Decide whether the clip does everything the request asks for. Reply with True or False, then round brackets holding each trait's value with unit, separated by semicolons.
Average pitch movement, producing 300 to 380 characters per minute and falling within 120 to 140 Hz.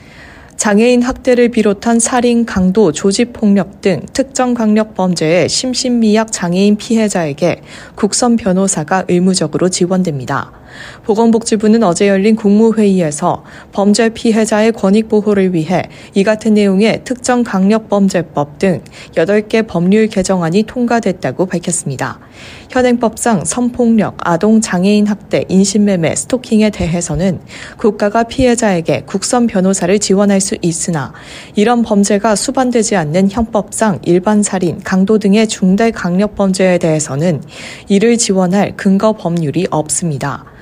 False (3.8 semitones; 305 characters per minute; 200 Hz)